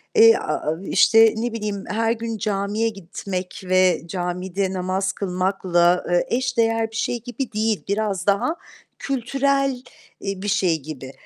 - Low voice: No, high, 200 Hz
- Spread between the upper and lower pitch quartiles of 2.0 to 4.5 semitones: Yes, average, 3.6 semitones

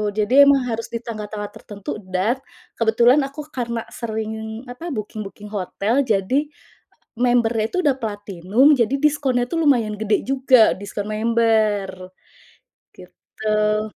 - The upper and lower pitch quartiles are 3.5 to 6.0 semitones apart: No, average, 3.0 semitones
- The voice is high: Yes, high, 220 Hz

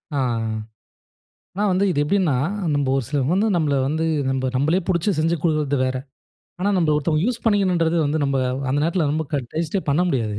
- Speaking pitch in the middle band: Yes, medium, 155 Hz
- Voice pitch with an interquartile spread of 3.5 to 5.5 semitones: Yes, average, 4.1 semitones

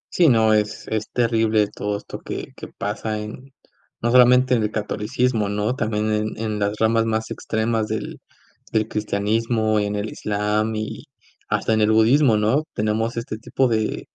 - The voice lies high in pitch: No, low, 110 Hz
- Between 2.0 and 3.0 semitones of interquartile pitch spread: No, narrow, 1.4 semitones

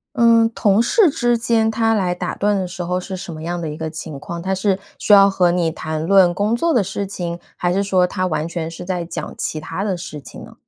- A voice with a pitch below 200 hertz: Yes, medium, 185 Hz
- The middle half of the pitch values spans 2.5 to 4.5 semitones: Yes, average, 3.3 semitones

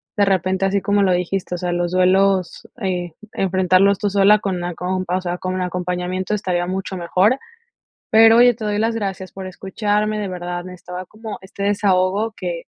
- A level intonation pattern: Yes, narrow, 2.0 semitones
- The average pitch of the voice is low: No, high, 190 Hz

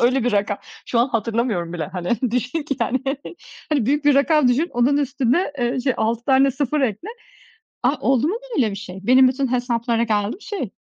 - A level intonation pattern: No, average, 3.4 semitones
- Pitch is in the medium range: No, very high, 250 Hz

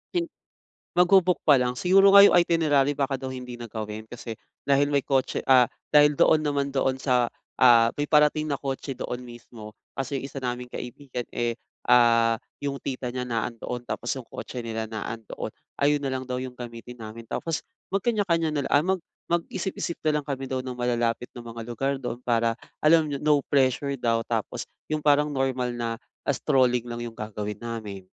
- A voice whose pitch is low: Yes, low, 130 Hz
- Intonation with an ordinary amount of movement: Yes, average, 3.4 semitones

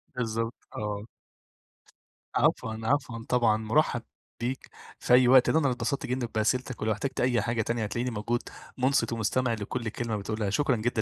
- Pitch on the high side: No, low, 120 Hz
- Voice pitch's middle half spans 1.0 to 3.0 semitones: Yes, narrow, 2.5 semitones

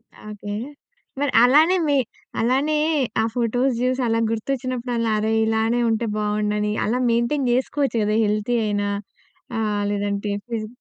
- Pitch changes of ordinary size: Yes, average, 3.2 semitones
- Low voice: No, high, 230 Hz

